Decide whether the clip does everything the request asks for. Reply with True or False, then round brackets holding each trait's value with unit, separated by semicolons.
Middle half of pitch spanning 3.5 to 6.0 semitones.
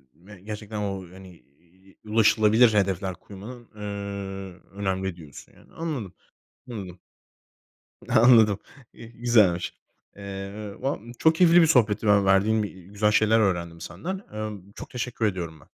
False (2.8 semitones)